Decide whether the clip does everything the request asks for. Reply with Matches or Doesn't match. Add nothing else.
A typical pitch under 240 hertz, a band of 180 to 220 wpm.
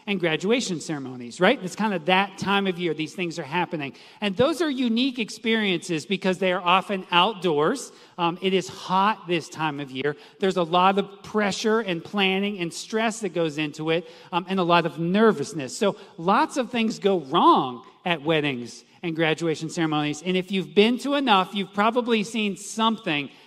Matches